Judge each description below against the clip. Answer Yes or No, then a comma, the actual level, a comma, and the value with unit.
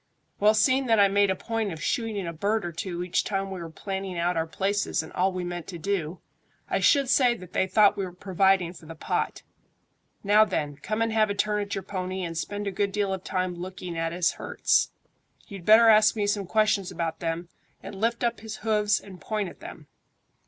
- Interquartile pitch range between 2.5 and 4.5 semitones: Yes, average, 3.1 semitones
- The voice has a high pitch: Yes, high, 195 Hz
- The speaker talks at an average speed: No, fast, 225 wpm